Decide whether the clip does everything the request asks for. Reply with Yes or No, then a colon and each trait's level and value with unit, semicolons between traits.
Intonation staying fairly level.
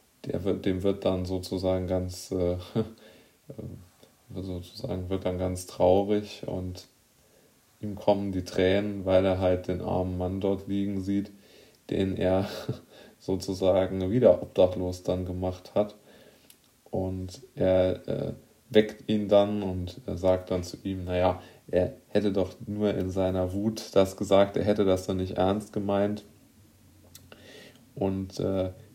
Yes: narrow, 2.1 semitones